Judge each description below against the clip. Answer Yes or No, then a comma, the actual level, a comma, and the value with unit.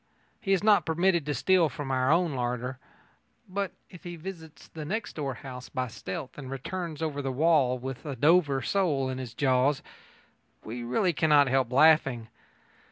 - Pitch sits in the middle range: Yes, medium, 145 Hz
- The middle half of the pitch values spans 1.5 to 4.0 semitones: No, average, 4.6 semitones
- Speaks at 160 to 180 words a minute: Yes, average, 170 wpm